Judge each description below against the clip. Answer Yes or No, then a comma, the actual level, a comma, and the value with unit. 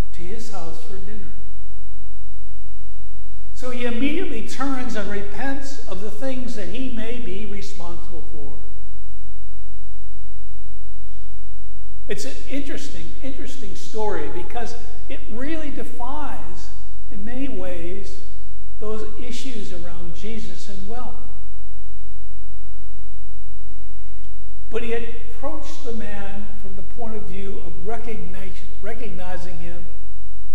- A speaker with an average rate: No, slow, 100 wpm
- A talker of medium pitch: No, low, 115 Hz